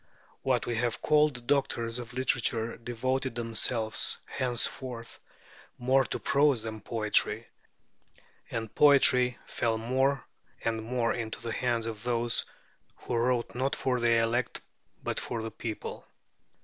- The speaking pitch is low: Yes, low, 120 Hz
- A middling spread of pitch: No, narrow, 1.9 semitones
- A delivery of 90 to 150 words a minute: Yes, slow, 135 wpm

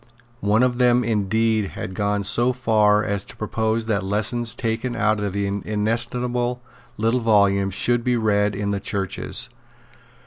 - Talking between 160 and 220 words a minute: No, average, 150 wpm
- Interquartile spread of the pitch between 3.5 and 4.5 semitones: No, average, 2.8 semitones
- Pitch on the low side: Yes, low, 110 Hz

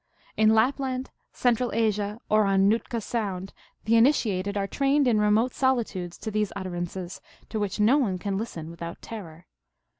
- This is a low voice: No, high, 210 Hz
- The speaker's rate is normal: Yes, average, 170 wpm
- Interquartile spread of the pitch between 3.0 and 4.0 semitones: Yes, average, 3.4 semitones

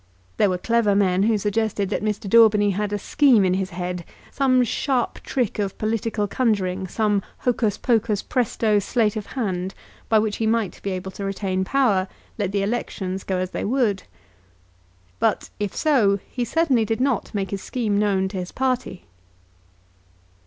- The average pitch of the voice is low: No, high, 210 Hz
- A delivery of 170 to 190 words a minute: Yes, average, 175 wpm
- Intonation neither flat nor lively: Yes, average, 3.2 semitones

